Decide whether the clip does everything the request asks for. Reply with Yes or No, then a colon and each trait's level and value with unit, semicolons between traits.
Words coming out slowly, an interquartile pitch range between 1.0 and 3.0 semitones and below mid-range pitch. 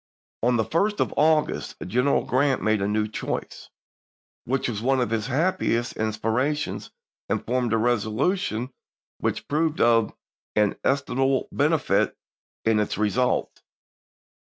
No: slow, 130 wpm; average, 4.1 semitones; low, 120 Hz